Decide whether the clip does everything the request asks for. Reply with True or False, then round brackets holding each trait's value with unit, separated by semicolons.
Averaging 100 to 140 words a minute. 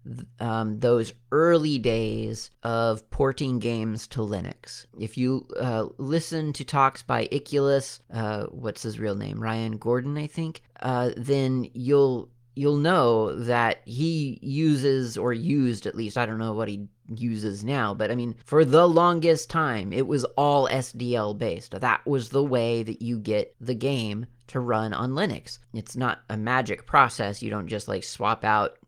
False (170 wpm)